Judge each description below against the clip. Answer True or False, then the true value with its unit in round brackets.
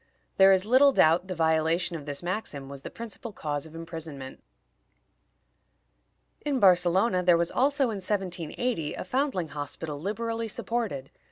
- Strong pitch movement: True (5.8 semitones)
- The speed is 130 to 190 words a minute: True (145 wpm)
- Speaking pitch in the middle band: True (180 Hz)